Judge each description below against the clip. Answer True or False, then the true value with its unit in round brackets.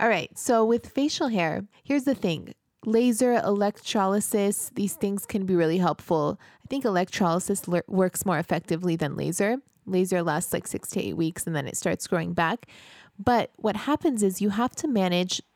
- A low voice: False (200 Hz)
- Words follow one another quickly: False (180 wpm)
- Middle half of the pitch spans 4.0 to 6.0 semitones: True (4.6 semitones)